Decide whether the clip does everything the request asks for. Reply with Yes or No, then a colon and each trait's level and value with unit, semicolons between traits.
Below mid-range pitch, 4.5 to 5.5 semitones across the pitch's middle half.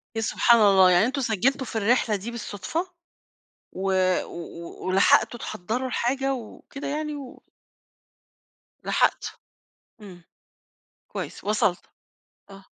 No: high, 220 Hz; average, 5.0 semitones